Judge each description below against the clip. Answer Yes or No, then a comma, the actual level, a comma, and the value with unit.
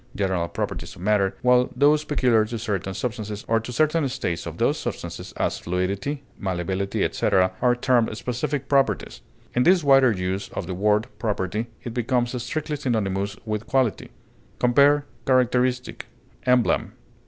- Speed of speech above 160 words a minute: No, average, 145 wpm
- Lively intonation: No, average, 4.5 semitones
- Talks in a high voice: No, low, 120 Hz